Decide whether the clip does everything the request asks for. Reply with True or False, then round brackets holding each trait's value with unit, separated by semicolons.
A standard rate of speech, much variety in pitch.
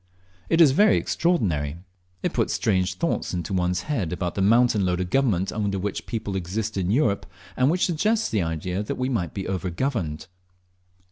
True (180 wpm; 6.2 semitones)